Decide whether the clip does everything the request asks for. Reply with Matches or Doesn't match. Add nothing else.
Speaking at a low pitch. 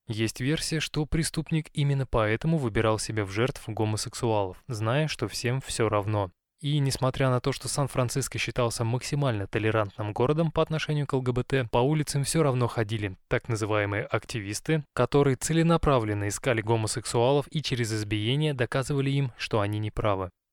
Matches